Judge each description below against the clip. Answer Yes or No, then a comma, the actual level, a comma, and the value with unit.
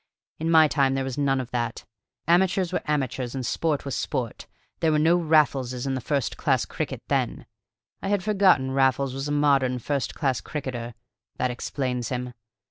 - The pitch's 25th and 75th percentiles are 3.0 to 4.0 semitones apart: Yes, average, 3.3 semitones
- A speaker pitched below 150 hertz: Yes, low, 135 Hz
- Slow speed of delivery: No, average, 175 wpm